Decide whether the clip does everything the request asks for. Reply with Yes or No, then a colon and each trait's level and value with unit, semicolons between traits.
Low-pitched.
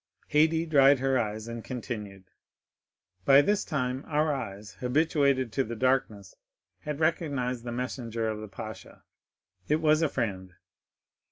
Yes: low, 125 Hz